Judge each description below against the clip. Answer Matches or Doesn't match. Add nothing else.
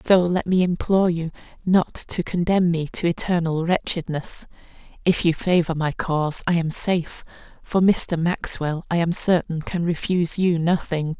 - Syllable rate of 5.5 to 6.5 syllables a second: Doesn't match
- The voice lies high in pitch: Doesn't match